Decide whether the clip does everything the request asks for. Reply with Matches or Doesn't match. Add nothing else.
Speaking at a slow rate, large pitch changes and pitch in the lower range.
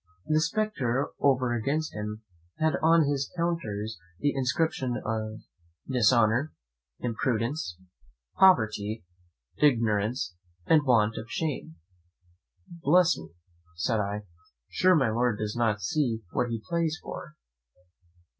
Matches